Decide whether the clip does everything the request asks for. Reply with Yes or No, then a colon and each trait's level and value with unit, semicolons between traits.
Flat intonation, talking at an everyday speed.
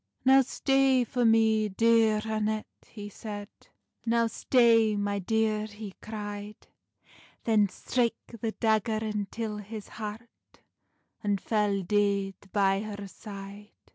No: narrow, 1.7 semitones; slow, 115 wpm